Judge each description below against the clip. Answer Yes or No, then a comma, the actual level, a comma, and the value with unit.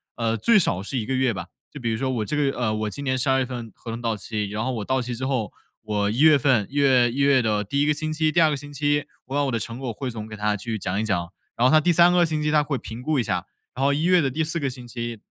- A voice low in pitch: Yes, low, 130 Hz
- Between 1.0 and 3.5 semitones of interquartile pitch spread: No, average, 4.4 semitones